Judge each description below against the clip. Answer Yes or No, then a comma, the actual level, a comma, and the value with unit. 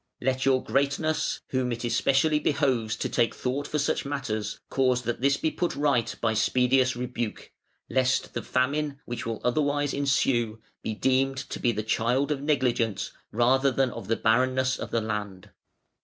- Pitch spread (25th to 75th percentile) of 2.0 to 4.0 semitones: Yes, average, 3.0 semitones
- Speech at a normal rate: Yes, average, 170 wpm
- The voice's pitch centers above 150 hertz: No, low, 130 Hz